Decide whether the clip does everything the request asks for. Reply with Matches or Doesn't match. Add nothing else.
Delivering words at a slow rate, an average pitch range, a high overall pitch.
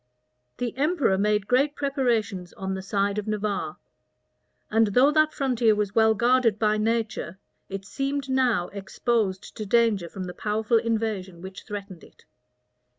Doesn't match